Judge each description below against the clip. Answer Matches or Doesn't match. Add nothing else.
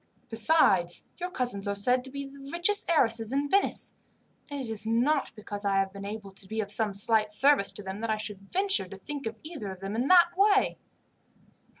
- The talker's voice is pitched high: Matches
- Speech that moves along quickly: Matches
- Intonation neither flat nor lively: Doesn't match